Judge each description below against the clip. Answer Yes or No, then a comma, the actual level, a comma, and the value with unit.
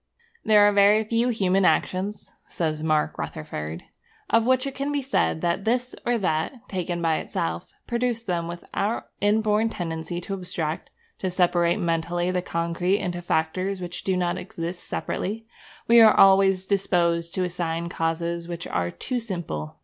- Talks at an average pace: Yes, average, 160 wpm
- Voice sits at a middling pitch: Yes, medium, 180 Hz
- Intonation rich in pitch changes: No, average, 3.8 semitones